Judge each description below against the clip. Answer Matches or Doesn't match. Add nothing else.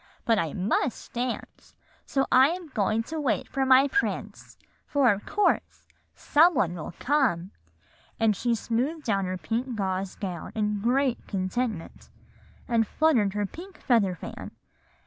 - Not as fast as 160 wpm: Matches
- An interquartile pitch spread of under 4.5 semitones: Doesn't match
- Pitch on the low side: Doesn't match